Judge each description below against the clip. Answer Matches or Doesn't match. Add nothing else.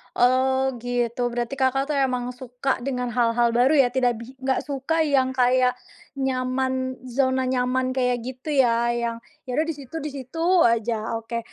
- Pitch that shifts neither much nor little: Doesn't match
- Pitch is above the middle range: Matches